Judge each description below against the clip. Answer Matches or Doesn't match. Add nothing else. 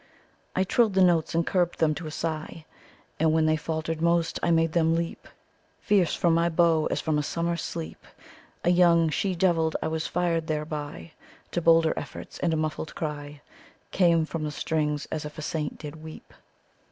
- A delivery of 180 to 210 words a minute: Matches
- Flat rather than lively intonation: Matches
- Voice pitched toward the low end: Doesn't match